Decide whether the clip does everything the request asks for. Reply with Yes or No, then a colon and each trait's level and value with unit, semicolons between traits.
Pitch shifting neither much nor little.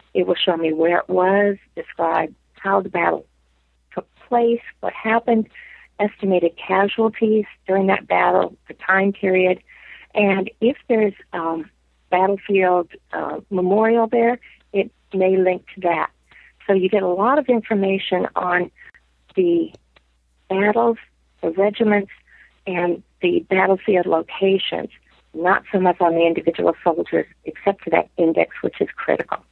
Yes: average, 3.4 semitones